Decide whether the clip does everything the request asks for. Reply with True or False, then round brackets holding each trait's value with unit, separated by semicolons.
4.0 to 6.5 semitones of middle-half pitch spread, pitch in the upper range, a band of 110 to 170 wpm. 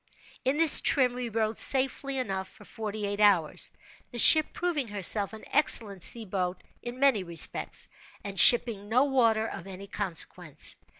True (4.4 semitones; 220 Hz; 155 wpm)